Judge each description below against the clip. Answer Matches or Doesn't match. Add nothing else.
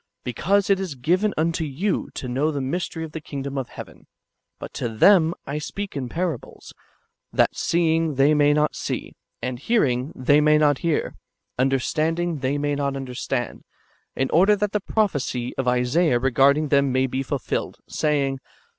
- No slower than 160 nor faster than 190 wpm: Matches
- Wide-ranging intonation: Doesn't match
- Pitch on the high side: Doesn't match